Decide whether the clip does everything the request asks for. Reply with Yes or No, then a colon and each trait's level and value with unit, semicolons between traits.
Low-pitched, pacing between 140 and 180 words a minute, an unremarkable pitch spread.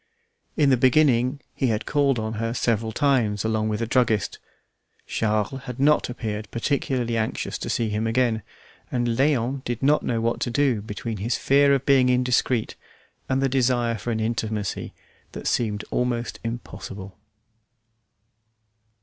Yes: low, 120 Hz; average, 150 wpm; average, 3.0 semitones